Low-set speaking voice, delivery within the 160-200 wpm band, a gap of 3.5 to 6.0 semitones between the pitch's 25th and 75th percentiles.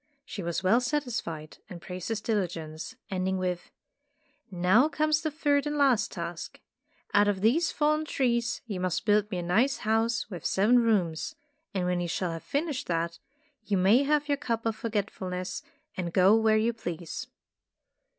No: high, 210 Hz; average, 170 wpm; wide, 5.5 semitones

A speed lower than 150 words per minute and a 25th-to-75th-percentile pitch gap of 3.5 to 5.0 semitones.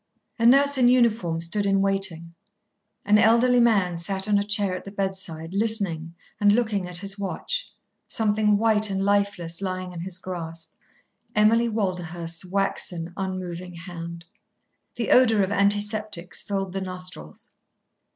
No: average, 140 wpm; average, 3.1 semitones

